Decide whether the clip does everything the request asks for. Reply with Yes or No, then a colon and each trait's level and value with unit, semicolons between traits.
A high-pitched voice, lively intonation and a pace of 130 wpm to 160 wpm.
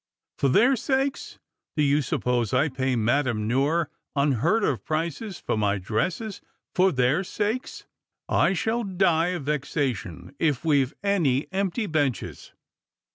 No: medium, 150 Hz; wide, 6.8 semitones; average, 140 wpm